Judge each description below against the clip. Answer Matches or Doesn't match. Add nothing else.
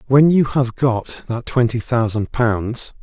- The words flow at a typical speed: Matches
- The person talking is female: Doesn't match